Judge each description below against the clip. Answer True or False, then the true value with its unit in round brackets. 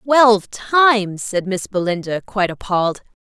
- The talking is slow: True (130 wpm)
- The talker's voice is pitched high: True (205 Hz)